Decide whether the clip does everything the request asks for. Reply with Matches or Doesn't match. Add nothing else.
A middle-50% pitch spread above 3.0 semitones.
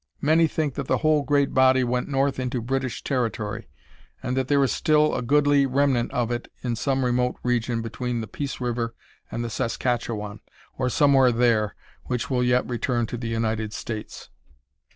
Doesn't match